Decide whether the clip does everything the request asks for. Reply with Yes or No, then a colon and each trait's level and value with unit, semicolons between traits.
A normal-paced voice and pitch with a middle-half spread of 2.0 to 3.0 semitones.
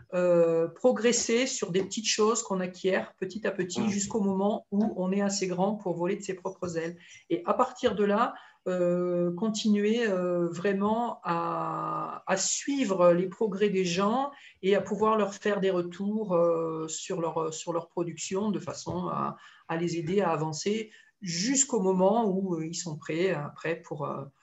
No: average, 175 wpm; average, 3.4 semitones